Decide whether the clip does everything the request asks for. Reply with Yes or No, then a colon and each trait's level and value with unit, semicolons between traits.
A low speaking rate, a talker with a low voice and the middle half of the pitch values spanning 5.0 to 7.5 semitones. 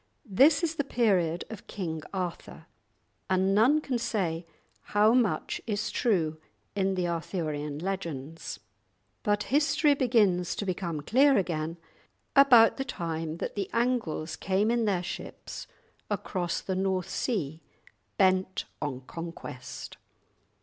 No: slow, 125 wpm; high, 190 Hz; wide, 5.4 semitones